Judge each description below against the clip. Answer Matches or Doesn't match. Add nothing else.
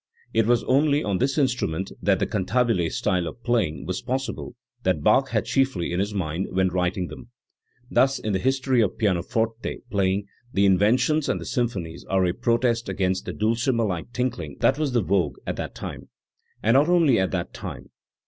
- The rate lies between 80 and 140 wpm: Doesn't match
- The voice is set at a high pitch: Doesn't match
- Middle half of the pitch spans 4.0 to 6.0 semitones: Matches